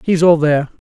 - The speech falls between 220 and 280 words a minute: No, fast, 205 wpm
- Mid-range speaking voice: Yes, medium, 160 Hz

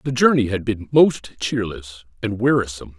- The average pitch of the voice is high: No, low, 115 Hz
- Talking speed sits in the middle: Yes, average, 160 wpm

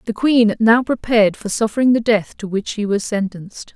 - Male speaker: No, female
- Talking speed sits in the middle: No, fast, 210 wpm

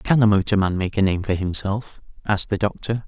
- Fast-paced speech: Yes, fast, 215 wpm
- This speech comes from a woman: No, male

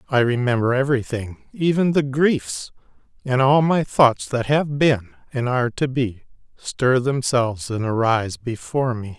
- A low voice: Yes, low, 125 Hz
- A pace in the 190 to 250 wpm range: No, average, 150 wpm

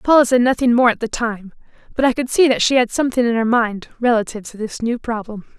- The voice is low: No, high, 235 Hz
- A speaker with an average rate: No, fast, 245 wpm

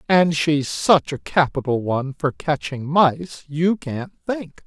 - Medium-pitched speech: Yes, medium, 150 Hz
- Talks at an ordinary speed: Yes, average, 155 wpm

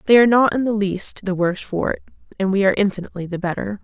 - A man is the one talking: No, female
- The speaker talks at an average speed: No, fast, 250 wpm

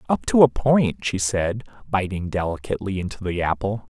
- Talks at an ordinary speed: Yes, average, 165 wpm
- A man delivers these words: Yes, male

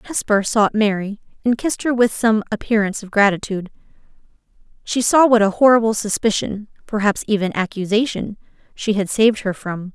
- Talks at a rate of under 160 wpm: Yes, average, 150 wpm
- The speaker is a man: No, female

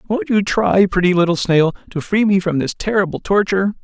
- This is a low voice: No, medium, 185 Hz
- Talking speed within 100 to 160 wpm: No, fast, 205 wpm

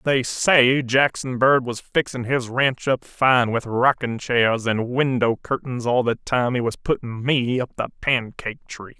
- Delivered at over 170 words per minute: Yes, average, 180 wpm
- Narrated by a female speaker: No, male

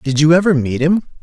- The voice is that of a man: Yes, male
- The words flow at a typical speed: No, fast, 245 wpm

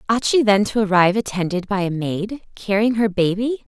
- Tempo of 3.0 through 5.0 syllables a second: No, 5.4 syllables/s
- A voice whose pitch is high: Yes, high, 205 Hz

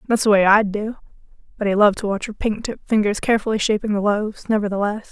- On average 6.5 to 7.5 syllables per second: Yes, 7.0 syllables/s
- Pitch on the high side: Yes, high, 210 Hz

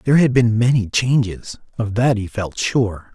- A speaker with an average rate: Yes, average, 190 wpm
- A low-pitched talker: Yes, low, 115 Hz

